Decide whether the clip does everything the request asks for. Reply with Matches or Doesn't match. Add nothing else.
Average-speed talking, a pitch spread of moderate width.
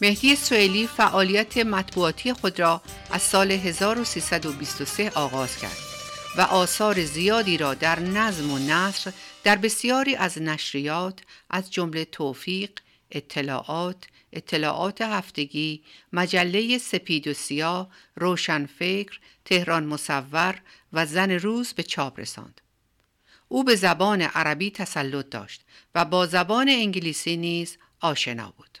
Matches